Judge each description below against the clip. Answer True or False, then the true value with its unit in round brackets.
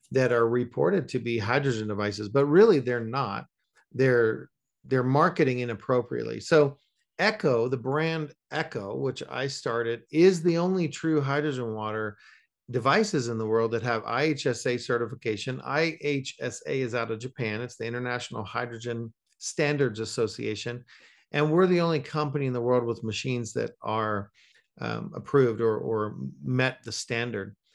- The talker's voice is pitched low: True (125 Hz)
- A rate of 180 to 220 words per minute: False (145 wpm)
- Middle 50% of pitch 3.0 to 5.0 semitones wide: True (3.7 semitones)